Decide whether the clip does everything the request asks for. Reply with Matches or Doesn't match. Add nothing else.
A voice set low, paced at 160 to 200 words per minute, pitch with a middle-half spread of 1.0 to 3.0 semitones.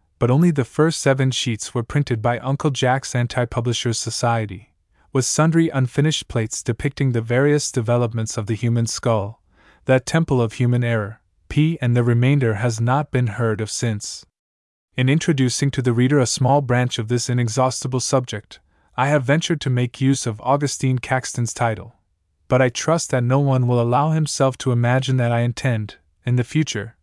Matches